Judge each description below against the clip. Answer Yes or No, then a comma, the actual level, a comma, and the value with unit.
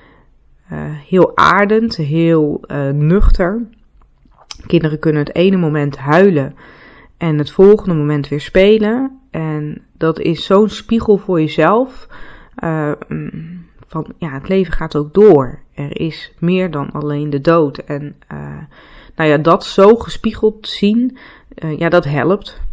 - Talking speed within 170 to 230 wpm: No, slow, 135 wpm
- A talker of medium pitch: Yes, medium, 165 Hz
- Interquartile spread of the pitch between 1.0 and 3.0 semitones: No, average, 5.1 semitones